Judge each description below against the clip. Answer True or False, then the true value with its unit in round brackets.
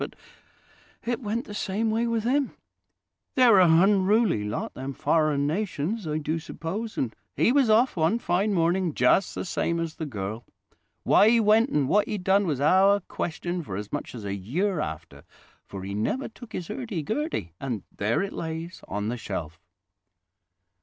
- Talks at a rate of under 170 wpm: False (180 wpm)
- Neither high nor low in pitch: True (175 Hz)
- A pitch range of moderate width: False (7.8 semitones)